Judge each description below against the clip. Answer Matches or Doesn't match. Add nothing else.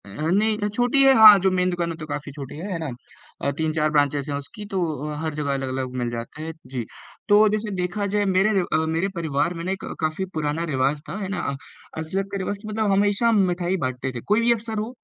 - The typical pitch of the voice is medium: Matches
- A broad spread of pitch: Matches